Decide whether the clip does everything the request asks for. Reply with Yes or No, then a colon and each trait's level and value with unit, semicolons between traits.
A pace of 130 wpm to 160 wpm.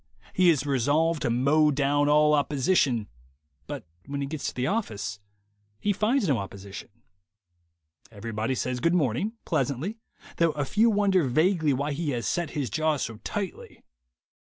Yes: average, 155 wpm